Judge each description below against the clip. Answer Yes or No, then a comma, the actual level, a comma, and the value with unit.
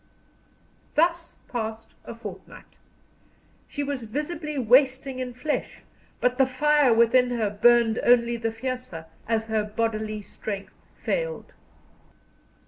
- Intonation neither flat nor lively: Yes, average, 3.6 semitones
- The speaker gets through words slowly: Yes, slow, 115 wpm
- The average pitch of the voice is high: Yes, high, 245 Hz